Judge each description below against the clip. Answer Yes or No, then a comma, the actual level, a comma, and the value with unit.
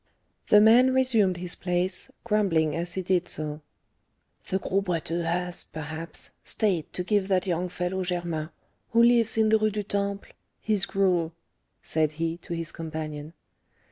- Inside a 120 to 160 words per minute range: Yes, average, 155 wpm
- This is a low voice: No, medium, 180 Hz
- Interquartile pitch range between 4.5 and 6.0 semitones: No, average, 3.5 semitones